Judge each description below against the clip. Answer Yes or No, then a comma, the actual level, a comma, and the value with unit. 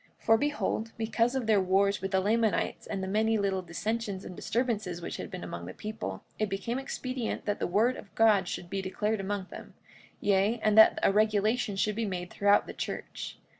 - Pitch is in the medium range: No, high, 210 Hz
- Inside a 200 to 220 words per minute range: Yes, fast, 205 wpm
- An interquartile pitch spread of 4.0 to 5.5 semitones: No, narrow, 2.6 semitones